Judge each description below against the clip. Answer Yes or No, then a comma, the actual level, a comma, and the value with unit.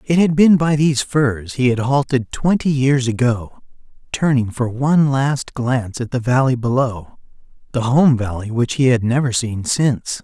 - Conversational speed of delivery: Yes, average, 175 wpm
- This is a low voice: Yes, low, 130 Hz